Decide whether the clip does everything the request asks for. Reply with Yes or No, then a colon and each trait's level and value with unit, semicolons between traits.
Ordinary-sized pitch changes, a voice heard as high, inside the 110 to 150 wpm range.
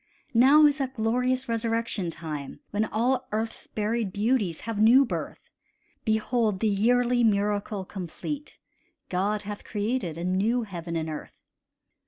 Yes: average, 3.8 semitones; high, 220 Hz; slow, 135 wpm